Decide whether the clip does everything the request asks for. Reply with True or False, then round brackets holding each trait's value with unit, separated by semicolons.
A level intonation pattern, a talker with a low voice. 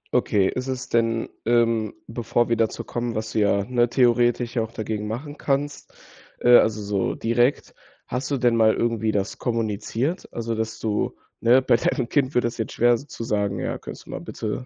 True (1.8 semitones; 115 Hz)